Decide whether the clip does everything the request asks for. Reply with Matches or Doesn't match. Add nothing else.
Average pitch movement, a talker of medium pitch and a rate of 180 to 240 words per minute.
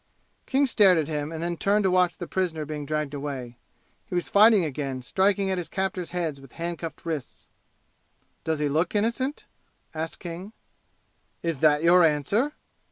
Doesn't match